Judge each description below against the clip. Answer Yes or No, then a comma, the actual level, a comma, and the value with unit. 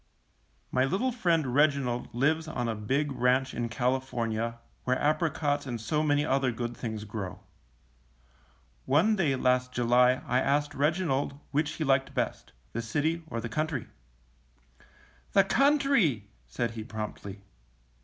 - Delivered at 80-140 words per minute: Yes, slow, 135 wpm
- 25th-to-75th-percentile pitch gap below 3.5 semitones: No, average, 4.3 semitones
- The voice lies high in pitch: No, low, 130 Hz